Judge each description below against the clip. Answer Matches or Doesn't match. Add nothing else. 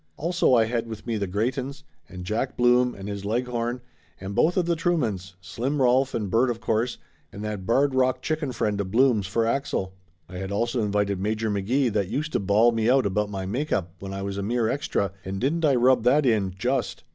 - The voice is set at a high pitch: Doesn't match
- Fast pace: Matches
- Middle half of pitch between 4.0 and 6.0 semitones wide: Matches